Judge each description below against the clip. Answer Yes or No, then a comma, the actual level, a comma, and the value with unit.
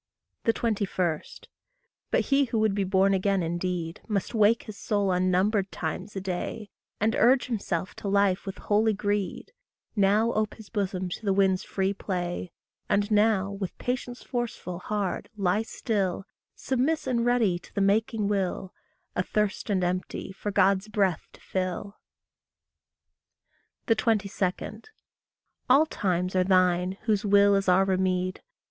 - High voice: Yes, high, 200 Hz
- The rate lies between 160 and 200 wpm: No, average, 140 wpm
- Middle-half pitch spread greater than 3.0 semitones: No, narrow, 2.6 semitones